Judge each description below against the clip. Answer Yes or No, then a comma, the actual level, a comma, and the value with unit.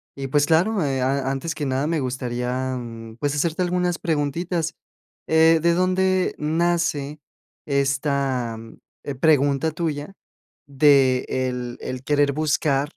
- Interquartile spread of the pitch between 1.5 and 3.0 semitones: No, average, 3.6 semitones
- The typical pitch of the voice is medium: Yes, medium, 145 Hz